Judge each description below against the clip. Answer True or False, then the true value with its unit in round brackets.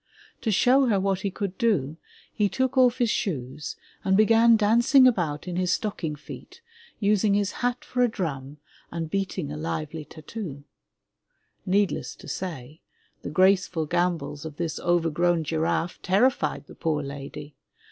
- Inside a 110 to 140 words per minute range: False (150 wpm)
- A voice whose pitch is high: False (180 Hz)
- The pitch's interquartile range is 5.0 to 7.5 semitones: True (5.3 semitones)